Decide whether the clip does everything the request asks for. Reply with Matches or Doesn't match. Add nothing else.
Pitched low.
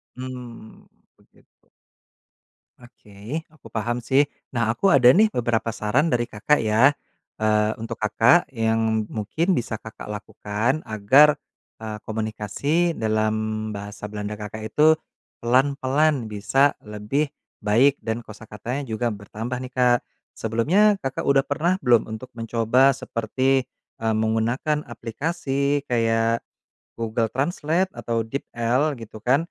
Matches